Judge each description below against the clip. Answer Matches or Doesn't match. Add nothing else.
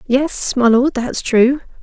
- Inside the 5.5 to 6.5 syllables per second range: Doesn't match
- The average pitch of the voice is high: Matches